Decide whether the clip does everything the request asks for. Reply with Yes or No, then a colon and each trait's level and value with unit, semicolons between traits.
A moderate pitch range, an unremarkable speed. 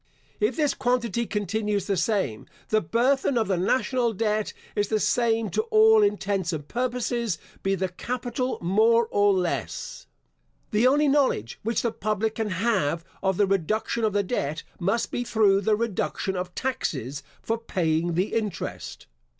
Yes: average, 4.1 semitones; average, 160 wpm